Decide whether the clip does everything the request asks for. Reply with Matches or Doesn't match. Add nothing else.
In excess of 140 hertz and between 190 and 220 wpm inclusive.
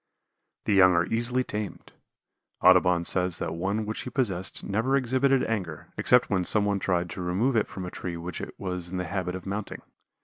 Doesn't match